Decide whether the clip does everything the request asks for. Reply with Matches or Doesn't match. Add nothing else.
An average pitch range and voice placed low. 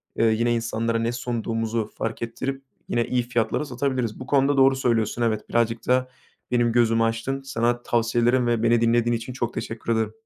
Doesn't match